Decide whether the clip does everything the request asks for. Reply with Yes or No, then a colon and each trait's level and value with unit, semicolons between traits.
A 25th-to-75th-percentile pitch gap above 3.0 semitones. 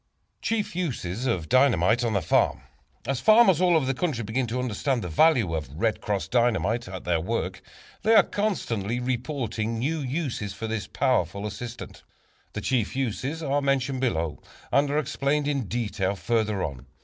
Yes: average, 5.2 semitones